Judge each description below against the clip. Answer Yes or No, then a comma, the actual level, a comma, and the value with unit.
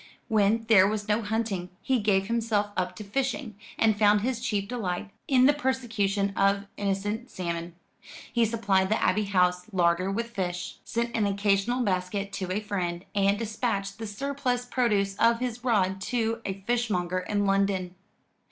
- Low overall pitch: No, high, 205 Hz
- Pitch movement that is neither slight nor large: Yes, average, 3.0 semitones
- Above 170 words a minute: No, average, 160 wpm